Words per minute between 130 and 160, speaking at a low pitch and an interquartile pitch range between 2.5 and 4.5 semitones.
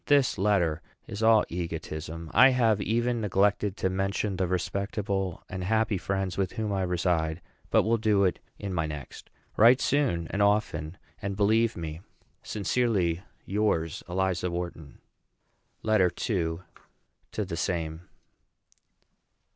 Yes: slow, 135 wpm; very low, 95 Hz; average, 3.8 semitones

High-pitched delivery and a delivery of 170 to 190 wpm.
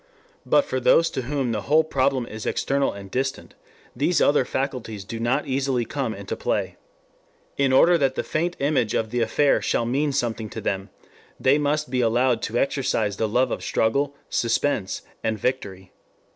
No: low, 130 Hz; average, 175 wpm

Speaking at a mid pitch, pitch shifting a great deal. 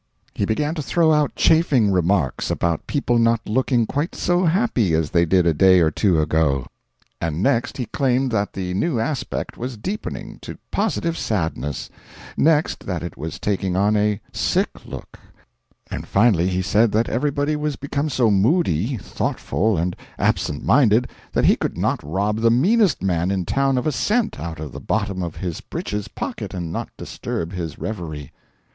No: low, 105 Hz; wide, 7.7 semitones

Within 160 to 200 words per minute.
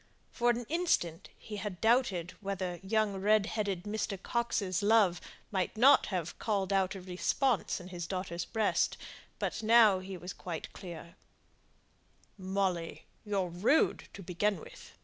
No: average, 145 wpm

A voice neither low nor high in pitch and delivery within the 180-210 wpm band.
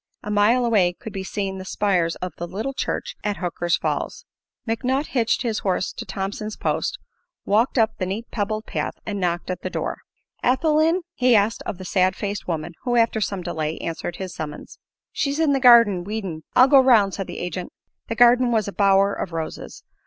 No: high, 205 Hz; average, 200 wpm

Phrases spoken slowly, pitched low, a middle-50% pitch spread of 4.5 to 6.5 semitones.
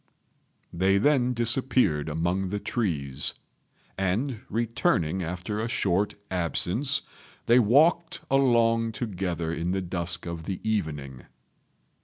Yes: slow, 110 wpm; very low, 95 Hz; wide, 5.5 semitones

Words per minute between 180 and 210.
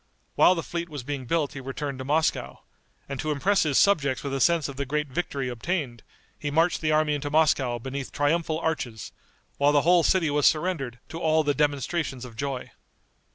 Yes: average, 200 wpm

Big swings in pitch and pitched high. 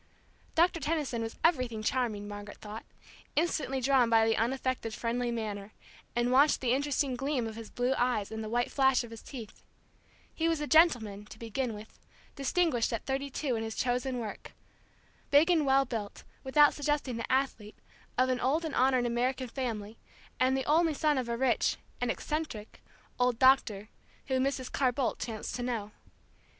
No: average, 3.3 semitones; very high, 250 Hz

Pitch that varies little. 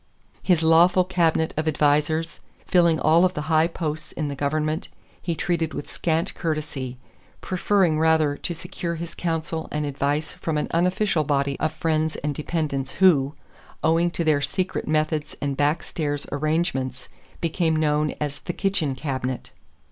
Yes: narrow, 2.2 semitones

